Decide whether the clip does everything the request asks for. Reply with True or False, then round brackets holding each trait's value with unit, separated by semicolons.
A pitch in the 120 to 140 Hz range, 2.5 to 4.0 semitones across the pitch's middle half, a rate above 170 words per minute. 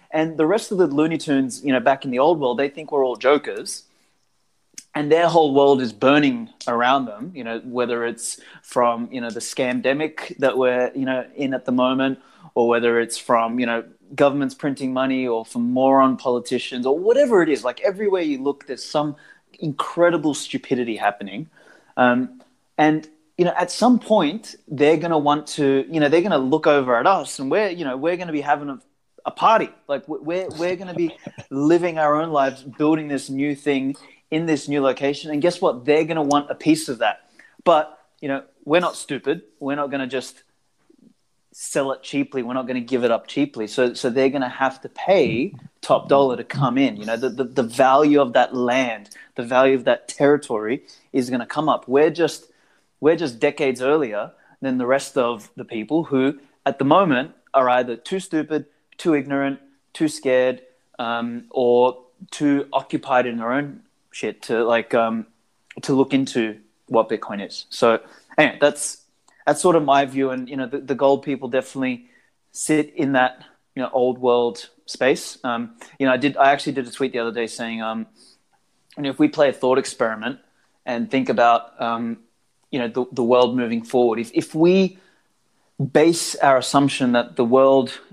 True (135 Hz; 3.0 semitones; 200 wpm)